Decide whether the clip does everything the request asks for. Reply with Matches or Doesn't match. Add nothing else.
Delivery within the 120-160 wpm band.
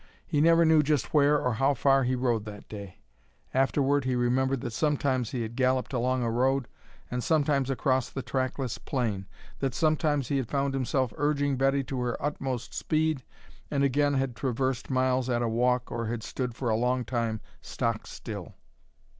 Doesn't match